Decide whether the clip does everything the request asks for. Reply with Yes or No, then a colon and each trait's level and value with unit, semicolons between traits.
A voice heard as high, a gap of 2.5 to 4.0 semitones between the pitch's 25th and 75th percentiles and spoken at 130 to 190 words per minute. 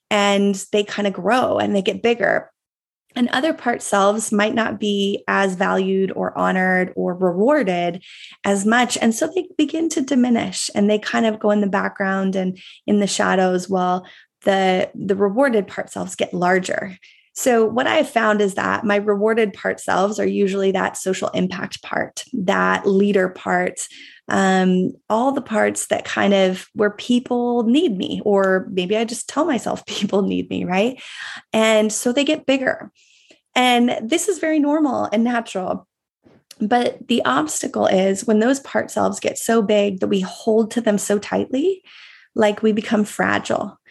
Yes: high, 210 Hz; average, 3.7 semitones; average, 170 wpm